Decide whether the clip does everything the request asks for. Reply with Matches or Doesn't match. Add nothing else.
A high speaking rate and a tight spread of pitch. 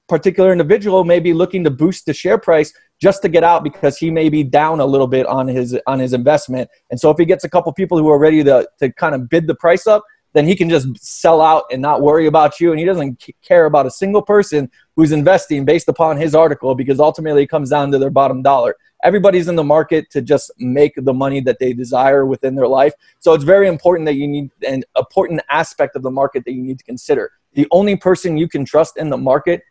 Doesn't match